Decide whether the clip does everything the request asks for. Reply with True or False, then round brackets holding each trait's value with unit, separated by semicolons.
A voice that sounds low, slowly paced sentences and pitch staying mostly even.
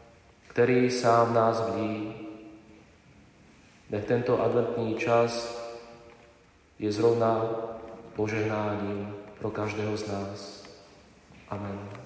True (110 Hz; 80 wpm; 1.9 semitones)